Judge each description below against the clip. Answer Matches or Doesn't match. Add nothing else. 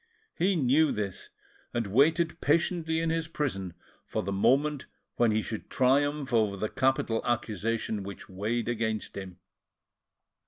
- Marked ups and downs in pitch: Matches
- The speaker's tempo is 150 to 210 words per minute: Doesn't match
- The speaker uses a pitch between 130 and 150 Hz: Doesn't match